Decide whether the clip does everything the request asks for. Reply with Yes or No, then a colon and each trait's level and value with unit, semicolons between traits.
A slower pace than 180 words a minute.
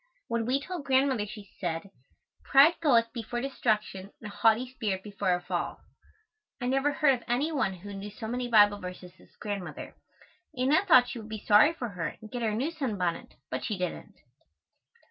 No: average, 190 wpm